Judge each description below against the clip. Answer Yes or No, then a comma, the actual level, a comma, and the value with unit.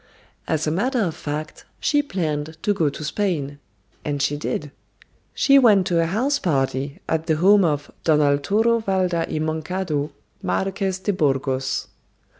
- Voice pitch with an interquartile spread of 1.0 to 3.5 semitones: No, average, 4.9 semitones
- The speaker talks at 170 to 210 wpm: No, average, 155 wpm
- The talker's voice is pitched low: No, medium, 160 Hz